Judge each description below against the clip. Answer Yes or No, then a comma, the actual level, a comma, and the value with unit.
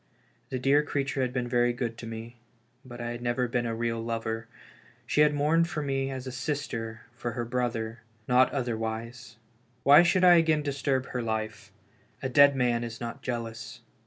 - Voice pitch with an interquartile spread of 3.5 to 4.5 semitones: No, average, 2.9 semitones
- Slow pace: No, average, 190 wpm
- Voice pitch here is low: Yes, low, 125 Hz